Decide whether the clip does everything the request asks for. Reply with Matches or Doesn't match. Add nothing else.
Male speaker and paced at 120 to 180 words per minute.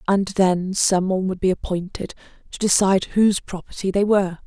Doesn't match